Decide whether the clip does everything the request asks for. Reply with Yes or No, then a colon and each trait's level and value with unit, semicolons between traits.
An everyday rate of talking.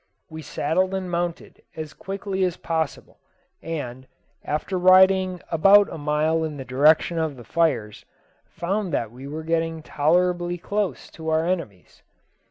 Yes: average, 145 wpm